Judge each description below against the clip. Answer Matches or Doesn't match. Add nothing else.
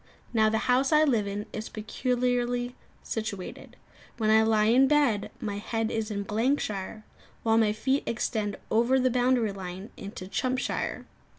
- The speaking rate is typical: Matches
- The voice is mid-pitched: Doesn't match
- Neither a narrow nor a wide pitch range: Matches